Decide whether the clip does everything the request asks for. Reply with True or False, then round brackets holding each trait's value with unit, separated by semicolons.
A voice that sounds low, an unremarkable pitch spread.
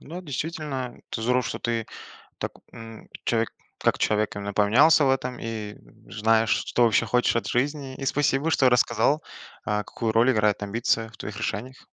True (120 Hz; 3.3 semitones)